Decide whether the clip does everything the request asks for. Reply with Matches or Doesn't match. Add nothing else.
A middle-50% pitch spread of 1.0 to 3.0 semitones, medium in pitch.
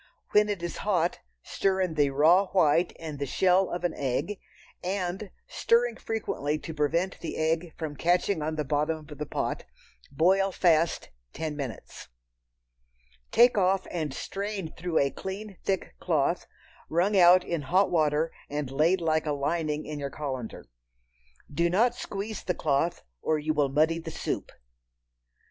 Doesn't match